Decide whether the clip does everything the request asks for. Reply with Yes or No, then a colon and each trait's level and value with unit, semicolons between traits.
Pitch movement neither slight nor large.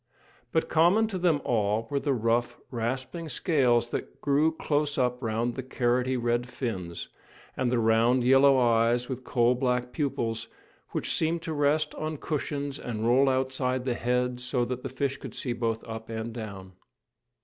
Yes: average, 3.0 semitones